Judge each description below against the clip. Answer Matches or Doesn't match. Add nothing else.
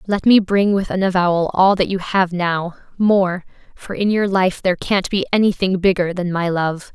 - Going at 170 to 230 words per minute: Matches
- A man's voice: Doesn't match